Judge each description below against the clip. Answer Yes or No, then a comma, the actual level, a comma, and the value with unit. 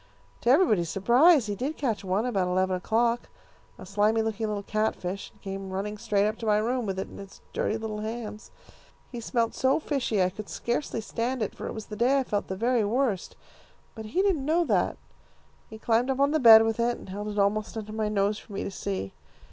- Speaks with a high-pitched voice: Yes, high, 220 Hz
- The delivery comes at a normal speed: No, fast, 225 wpm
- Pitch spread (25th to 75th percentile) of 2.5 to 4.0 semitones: Yes, average, 3.0 semitones